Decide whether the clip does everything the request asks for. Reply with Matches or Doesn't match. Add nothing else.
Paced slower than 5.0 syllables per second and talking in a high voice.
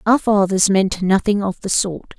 Matches